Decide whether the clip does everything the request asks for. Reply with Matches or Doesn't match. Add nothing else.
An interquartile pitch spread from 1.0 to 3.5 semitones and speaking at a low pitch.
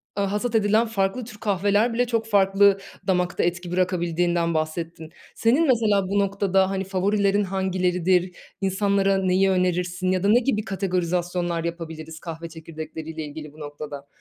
Doesn't match